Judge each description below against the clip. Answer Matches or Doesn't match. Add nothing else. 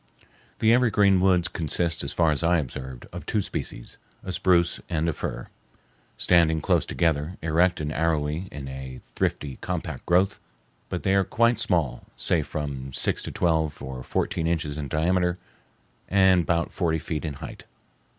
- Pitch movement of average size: Matches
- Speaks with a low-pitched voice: Matches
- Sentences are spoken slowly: Doesn't match